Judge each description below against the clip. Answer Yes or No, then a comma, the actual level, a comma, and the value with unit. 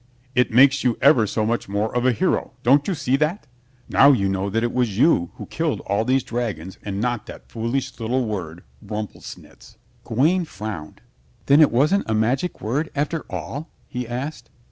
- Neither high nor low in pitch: No, low, 120 Hz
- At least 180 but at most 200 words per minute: Yes, average, 185 wpm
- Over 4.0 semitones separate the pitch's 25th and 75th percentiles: Yes, average, 4.5 semitones